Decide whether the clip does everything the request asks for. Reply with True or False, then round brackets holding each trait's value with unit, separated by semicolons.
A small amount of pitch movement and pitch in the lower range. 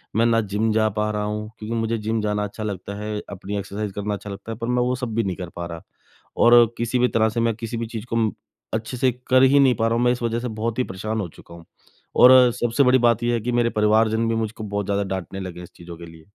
True (2.3 semitones; 110 Hz)